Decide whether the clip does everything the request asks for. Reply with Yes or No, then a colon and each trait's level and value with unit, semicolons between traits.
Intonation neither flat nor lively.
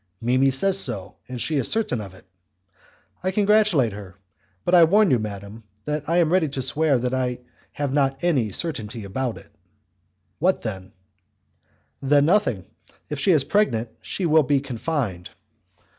No: wide, 6.3 semitones